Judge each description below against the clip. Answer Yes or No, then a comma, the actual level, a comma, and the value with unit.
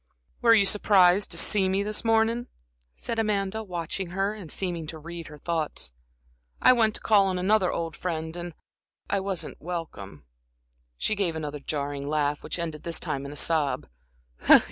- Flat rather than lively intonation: No, average, 4.3 semitones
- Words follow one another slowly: No, average, 170 wpm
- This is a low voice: No, medium, 175 Hz